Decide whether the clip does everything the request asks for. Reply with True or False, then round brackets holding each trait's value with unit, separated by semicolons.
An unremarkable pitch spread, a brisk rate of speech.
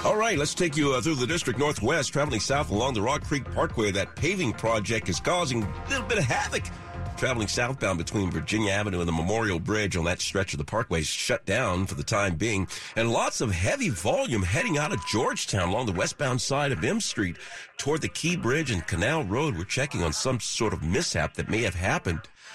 False (6.3 semitones; 220 wpm)